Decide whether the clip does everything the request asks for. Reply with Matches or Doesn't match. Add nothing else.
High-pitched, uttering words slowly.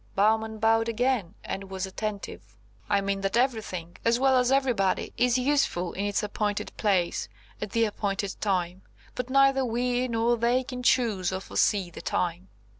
Doesn't match